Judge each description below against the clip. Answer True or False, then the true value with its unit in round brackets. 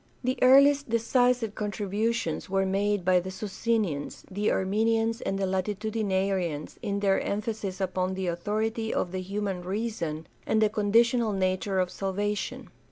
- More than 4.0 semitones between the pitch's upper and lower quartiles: False (2.9 semitones)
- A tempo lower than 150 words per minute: True (140 wpm)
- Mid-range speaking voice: False (205 Hz)